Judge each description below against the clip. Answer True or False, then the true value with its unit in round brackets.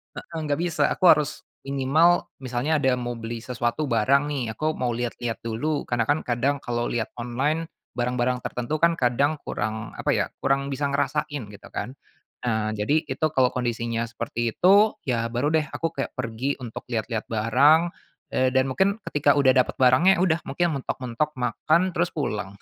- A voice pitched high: False (130 Hz)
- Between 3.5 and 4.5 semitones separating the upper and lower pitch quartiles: True (4.2 semitones)